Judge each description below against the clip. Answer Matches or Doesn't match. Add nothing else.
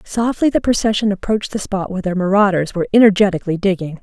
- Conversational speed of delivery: Matches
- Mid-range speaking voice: Doesn't match